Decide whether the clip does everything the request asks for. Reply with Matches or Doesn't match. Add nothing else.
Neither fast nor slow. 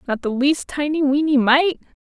Matches